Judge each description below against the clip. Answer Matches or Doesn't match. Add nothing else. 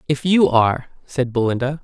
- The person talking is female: Doesn't match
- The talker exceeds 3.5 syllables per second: Matches